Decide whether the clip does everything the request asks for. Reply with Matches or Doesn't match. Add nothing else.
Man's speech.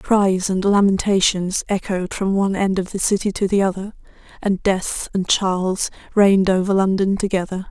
Doesn't match